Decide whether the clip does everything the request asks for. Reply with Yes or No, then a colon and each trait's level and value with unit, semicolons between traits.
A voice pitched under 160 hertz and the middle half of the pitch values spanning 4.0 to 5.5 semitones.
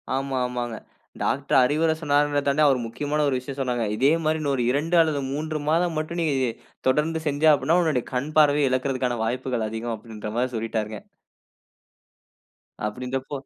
No: low, 135 Hz; average, 3.4 semitones